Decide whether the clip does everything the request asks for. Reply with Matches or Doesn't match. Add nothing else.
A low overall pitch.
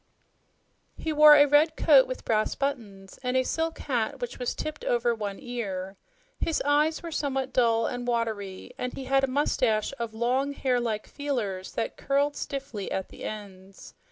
Doesn't match